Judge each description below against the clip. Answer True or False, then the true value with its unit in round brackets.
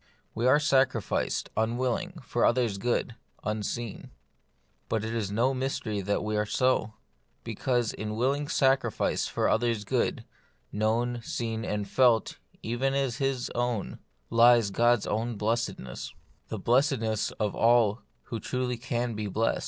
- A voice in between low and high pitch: False (115 Hz)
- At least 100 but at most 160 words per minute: True (140 wpm)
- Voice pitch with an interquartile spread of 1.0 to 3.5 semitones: True (2.7 semitones)